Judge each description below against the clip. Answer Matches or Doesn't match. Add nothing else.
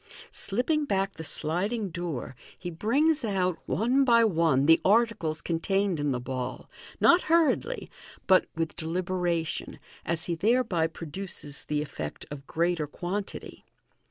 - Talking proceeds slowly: Matches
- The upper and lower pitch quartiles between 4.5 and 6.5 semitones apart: Matches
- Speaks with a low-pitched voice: Doesn't match